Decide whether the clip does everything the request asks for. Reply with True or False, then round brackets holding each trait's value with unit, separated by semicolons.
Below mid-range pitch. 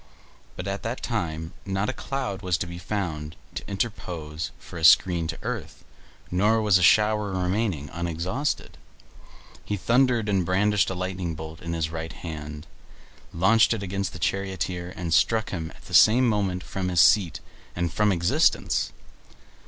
True (90 Hz)